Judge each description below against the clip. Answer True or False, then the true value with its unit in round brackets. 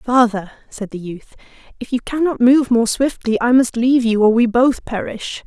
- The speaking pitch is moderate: False (235 Hz)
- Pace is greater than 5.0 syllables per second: False (4.9 syllables/s)